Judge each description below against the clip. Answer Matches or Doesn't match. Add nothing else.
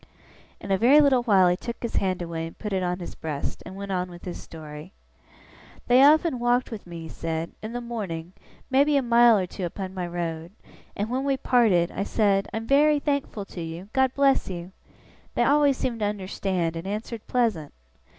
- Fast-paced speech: Matches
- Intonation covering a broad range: Matches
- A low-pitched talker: Doesn't match